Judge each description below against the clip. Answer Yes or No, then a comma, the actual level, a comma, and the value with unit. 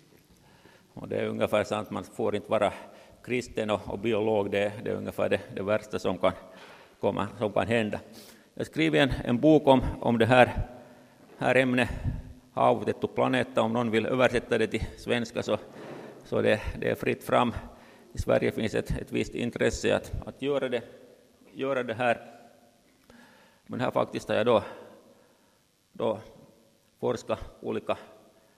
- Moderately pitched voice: No, low, 115 Hz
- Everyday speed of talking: Yes, average, 165 wpm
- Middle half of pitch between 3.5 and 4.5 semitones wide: No, average, 2.9 semitones